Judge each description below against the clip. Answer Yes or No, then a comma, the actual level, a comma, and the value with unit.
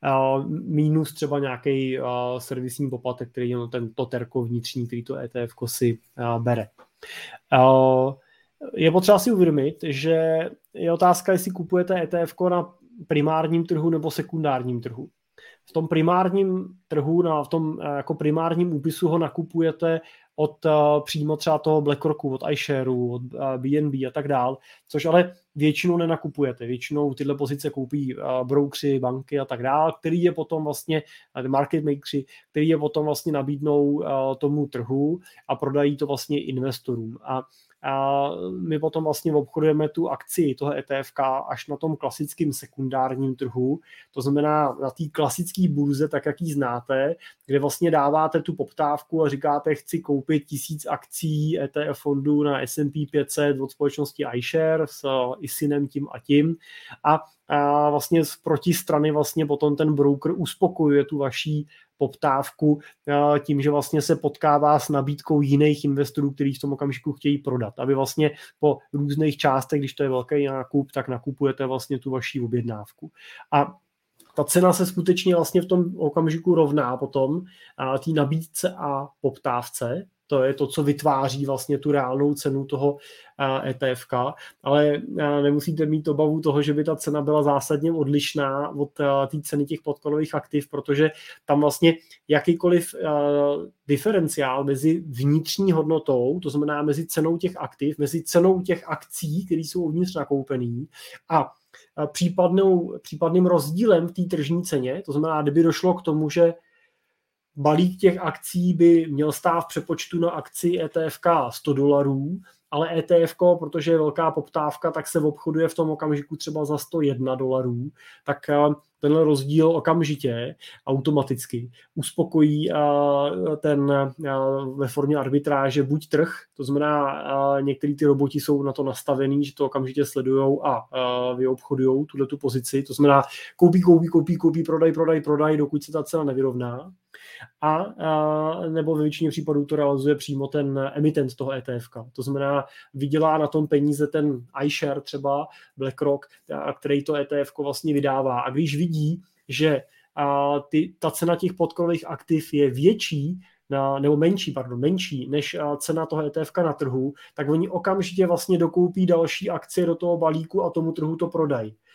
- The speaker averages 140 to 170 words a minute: Yes, average, 150 wpm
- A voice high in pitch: No, medium, 150 Hz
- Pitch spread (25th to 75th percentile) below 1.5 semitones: No, narrow, 2.6 semitones